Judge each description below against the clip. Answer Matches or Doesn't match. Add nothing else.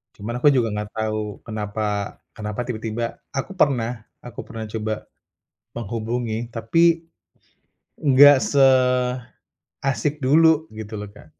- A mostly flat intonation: Doesn't match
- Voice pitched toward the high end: Doesn't match